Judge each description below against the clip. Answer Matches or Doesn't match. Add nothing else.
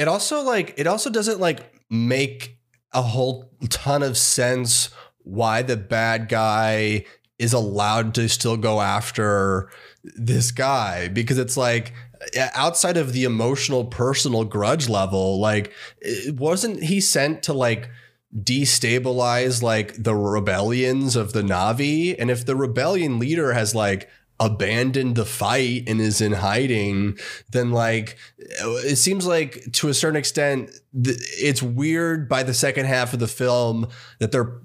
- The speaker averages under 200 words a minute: Matches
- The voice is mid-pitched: Doesn't match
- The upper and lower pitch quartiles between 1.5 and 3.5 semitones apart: Matches